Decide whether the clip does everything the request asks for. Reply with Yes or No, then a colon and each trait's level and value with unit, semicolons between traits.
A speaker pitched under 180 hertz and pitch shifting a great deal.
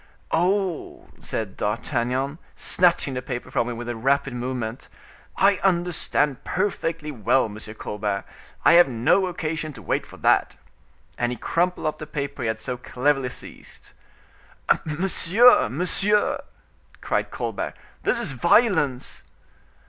Yes: medium, 140 Hz; wide, 6.1 semitones